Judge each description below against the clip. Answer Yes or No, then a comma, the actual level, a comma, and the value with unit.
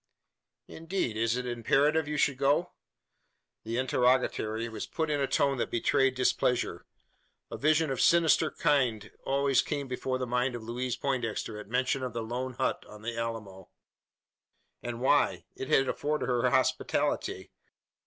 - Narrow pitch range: No, average, 3.2 semitones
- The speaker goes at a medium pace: Yes, average, 155 wpm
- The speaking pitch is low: Yes, low, 130 Hz